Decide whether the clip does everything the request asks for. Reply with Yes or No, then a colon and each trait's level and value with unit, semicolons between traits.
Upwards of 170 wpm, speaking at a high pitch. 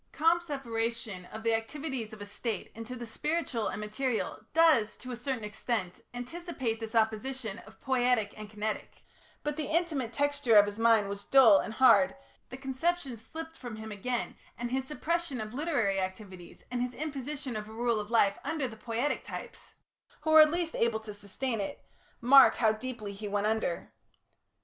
Yes: average, 180 wpm; high, 235 Hz